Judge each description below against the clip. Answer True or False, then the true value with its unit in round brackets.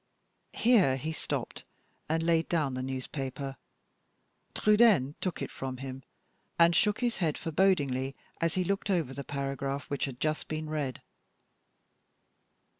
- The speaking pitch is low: False (155 Hz)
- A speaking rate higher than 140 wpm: False (135 wpm)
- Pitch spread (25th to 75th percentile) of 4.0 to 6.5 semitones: True (4.3 semitones)